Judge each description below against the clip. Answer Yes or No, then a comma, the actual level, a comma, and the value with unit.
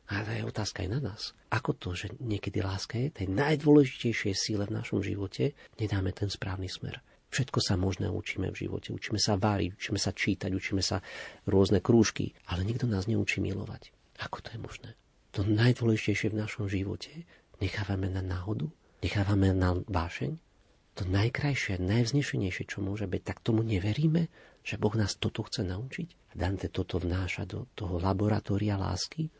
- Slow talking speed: No, fast, 165 wpm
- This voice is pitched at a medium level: No, low, 105 Hz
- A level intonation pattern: No, average, 3.0 semitones